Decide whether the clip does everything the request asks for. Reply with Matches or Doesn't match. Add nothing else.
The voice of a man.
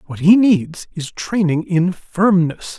Matches